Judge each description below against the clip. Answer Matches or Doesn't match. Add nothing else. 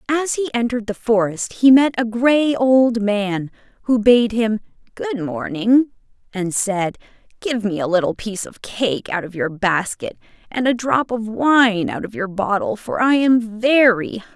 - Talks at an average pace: Matches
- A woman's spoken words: Matches